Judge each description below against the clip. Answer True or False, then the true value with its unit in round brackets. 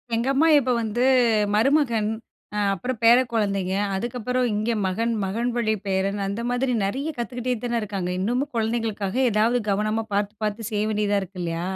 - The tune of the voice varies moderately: True (3.3 semitones)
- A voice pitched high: True (220 Hz)